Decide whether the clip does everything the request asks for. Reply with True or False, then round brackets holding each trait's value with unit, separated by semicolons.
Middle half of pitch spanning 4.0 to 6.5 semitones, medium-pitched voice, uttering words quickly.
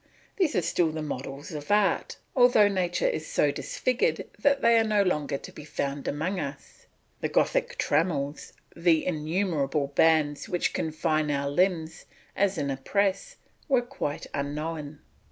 False (5.2 semitones; 160 Hz; 155 wpm)